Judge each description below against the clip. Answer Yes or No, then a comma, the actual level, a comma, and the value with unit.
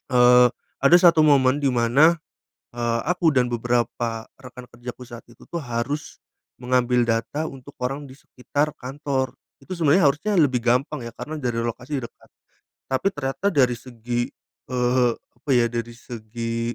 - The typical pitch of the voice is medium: No, low, 125 Hz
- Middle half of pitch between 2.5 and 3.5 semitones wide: Yes, average, 3.1 semitones